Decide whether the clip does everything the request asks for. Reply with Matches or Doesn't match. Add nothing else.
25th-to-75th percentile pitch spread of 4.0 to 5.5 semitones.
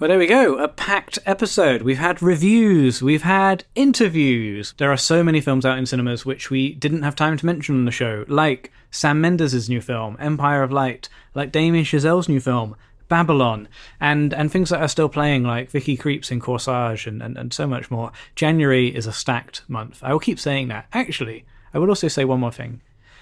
Matches